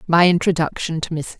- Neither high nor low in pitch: Yes, medium, 165 Hz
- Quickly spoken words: No, average, 170 wpm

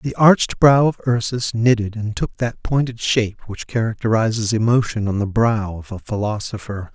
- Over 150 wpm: Yes, average, 175 wpm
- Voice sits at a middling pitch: No, low, 115 Hz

